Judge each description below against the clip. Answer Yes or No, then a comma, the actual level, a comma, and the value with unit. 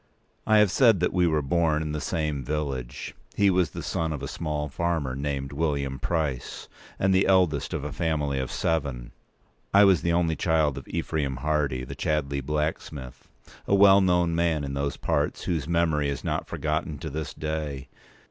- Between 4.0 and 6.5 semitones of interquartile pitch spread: No, average, 3.4 semitones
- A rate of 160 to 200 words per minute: Yes, average, 180 wpm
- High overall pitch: No, very low, 75 Hz